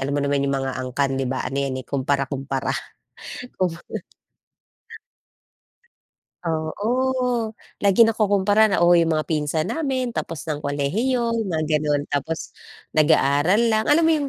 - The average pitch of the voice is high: No, medium, 160 Hz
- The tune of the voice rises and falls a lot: Yes, wide, 7.5 semitones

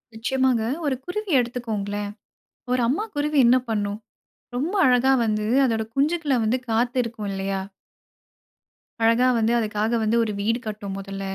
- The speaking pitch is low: No, high, 230 Hz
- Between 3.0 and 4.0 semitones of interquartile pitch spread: Yes, average, 3.5 semitones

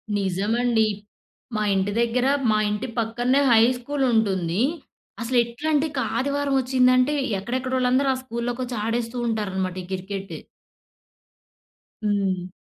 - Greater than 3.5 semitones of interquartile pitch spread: Yes, average, 3.9 semitones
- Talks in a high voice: Yes, high, 235 Hz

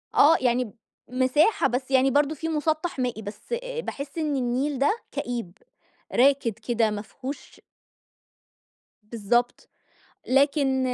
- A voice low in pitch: No, very high, 260 Hz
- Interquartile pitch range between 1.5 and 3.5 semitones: Yes, average, 3.2 semitones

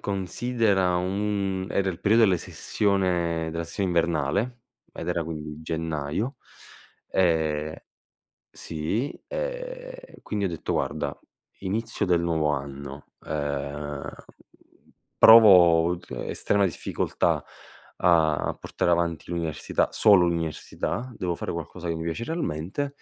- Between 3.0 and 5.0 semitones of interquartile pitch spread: Yes, average, 4.2 semitones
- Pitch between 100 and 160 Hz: No, very low, 85 Hz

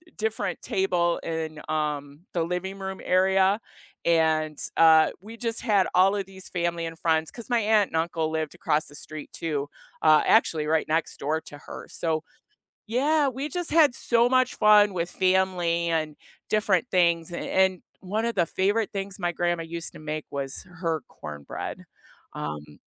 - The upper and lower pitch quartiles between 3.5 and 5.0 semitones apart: Yes, average, 4.2 semitones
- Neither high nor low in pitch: Yes, medium, 175 Hz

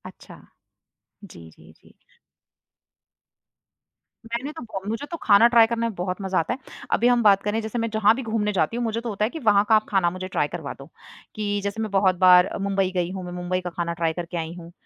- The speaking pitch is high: Yes, high, 200 Hz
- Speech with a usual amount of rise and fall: Yes, average, 4.0 semitones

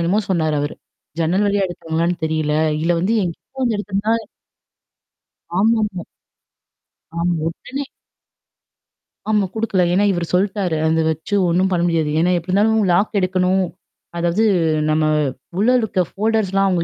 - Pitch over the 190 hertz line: No, medium, 185 Hz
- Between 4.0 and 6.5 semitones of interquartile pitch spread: No, average, 3.5 semitones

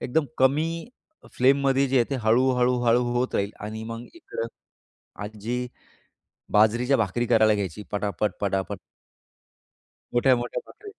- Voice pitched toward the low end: Yes, low, 120 Hz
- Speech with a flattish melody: No, average, 3.5 semitones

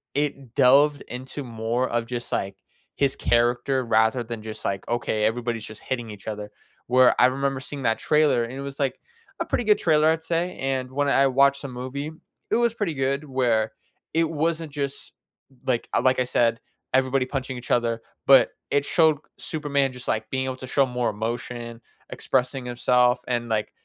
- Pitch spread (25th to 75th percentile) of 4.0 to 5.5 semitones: No, average, 2.8 semitones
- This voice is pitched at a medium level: No, low, 130 Hz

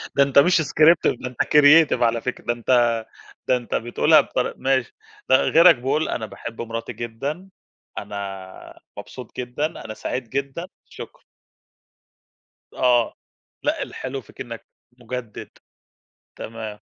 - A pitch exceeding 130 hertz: No, low, 125 Hz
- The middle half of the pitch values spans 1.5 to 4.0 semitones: Yes, average, 3.6 semitones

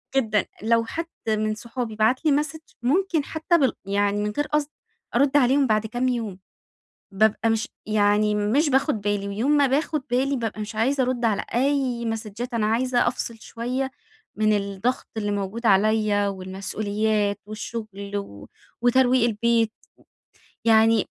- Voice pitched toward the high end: Yes, high, 225 Hz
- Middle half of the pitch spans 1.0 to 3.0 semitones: No, average, 3.7 semitones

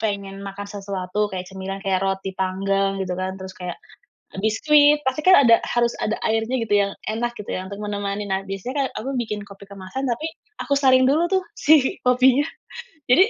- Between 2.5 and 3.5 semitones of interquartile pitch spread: No, average, 4.5 semitones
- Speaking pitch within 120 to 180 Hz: No, high, 205 Hz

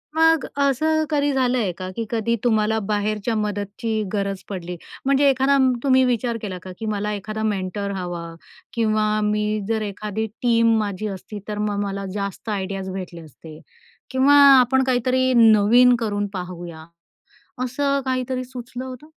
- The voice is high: Yes, high, 215 Hz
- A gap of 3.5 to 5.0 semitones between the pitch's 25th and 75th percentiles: Yes, average, 4.1 semitones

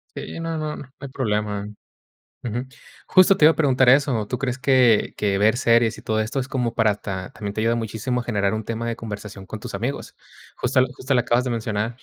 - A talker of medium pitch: No, low, 115 Hz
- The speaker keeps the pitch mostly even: No, average, 3.4 semitones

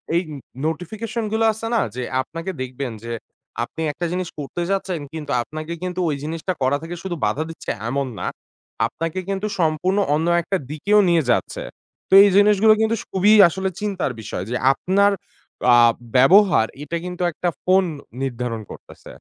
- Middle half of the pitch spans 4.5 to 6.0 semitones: Yes, average, 4.8 semitones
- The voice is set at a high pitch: No, medium, 175 Hz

